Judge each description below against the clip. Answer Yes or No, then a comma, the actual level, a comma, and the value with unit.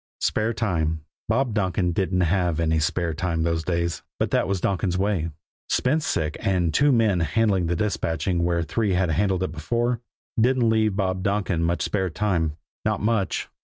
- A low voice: Yes, very low, 95 Hz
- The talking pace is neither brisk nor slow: Yes, average, 170 wpm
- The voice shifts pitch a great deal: No, average, 4.1 semitones